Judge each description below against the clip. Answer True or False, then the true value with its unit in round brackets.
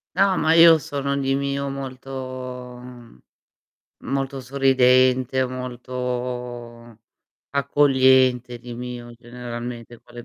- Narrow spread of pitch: True (1.8 semitones)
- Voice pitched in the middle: False (125 Hz)